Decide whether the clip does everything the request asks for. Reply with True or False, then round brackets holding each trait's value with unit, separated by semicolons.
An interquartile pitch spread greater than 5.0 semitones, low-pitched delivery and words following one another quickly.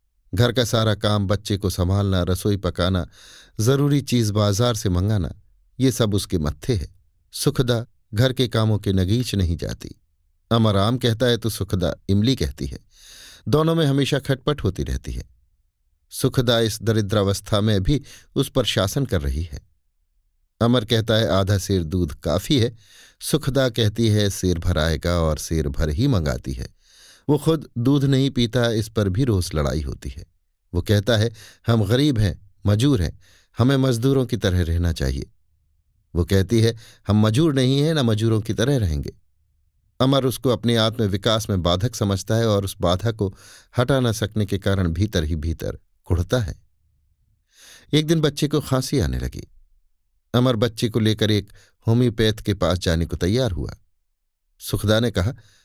False (5.6 semitones; 105 Hz; 165 wpm)